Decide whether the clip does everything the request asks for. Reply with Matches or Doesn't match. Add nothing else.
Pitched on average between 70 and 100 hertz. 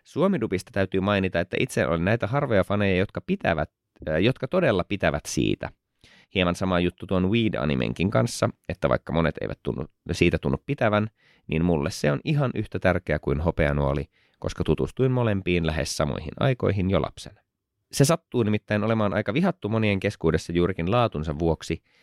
Matches